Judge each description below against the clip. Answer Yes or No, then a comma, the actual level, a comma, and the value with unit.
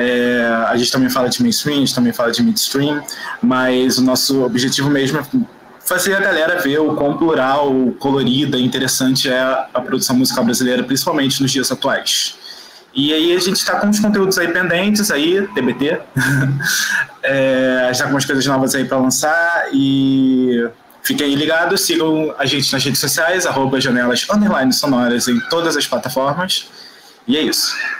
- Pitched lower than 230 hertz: Yes, low, 135 Hz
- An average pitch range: Yes, average, 4.6 semitones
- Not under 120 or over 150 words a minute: No, average, 170 wpm